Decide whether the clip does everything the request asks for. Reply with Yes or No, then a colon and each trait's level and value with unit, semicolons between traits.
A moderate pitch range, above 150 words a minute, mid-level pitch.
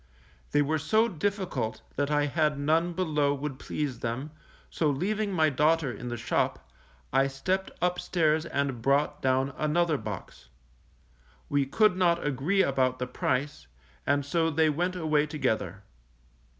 No: average, 3.8 semitones; average, 145 wpm; medium, 150 Hz